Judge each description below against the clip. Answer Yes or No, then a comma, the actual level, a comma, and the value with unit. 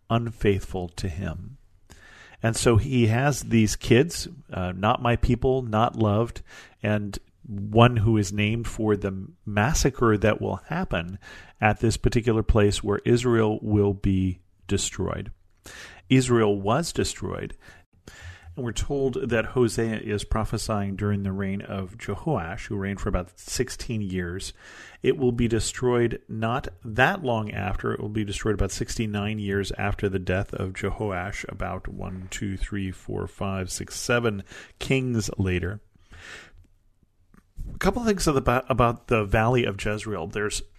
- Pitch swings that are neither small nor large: Yes, average, 3.2 semitones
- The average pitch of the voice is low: Yes, low, 105 Hz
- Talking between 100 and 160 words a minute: Yes, average, 140 wpm